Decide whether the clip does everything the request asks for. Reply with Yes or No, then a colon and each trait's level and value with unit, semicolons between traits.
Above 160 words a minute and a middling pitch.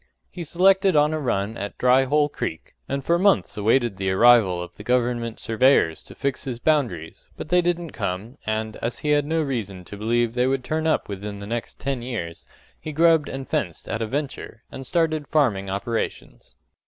No: average, 195 wpm; low, 125 Hz